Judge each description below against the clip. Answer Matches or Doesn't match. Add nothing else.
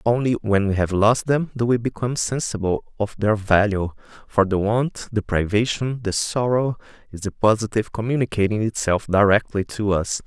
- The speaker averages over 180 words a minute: Doesn't match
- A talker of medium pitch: Doesn't match